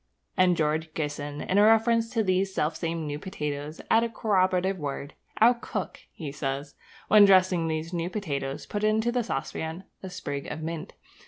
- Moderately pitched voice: Yes, medium, 175 Hz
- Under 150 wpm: No, average, 170 wpm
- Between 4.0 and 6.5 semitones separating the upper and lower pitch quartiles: Yes, average, 5.3 semitones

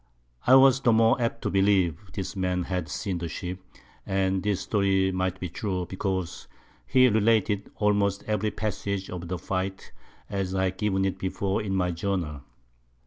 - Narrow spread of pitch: Yes, narrow, 1.9 semitones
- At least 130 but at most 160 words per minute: No, average, 170 wpm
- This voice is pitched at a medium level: No, very low, 95 Hz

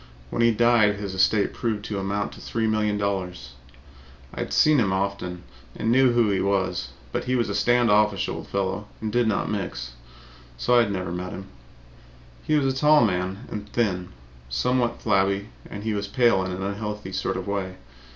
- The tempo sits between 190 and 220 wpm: Yes, average, 200 wpm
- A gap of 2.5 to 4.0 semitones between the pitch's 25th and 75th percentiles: Yes, average, 3.4 semitones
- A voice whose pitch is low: Yes, low, 100 Hz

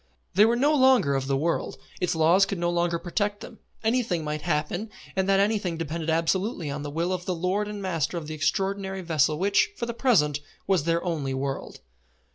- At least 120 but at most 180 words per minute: No, fast, 205 wpm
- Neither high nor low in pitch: Yes, medium, 175 Hz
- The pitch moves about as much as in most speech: Yes, average, 4.2 semitones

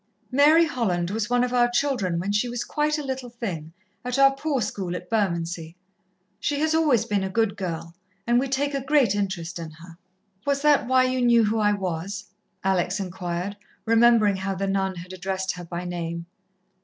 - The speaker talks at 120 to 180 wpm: No, average, 195 wpm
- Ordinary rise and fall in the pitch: No, wide, 6.0 semitones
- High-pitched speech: Yes, high, 205 Hz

